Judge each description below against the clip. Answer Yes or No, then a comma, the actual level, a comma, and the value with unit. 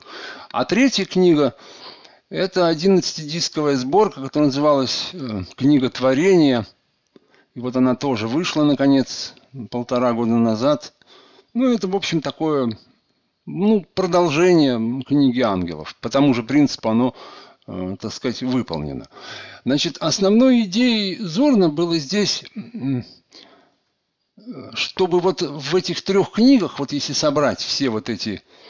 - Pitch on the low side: No, medium, 150 Hz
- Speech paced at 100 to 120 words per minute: Yes, average, 115 wpm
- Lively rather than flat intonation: Yes, wide, 6.7 semitones